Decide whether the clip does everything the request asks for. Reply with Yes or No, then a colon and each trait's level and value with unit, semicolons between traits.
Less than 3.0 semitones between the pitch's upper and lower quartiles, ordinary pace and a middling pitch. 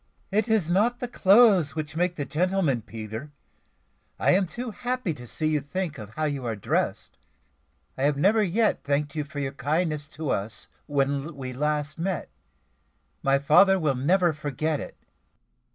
No: average, 5.0 semitones; average, 170 wpm; medium, 155 Hz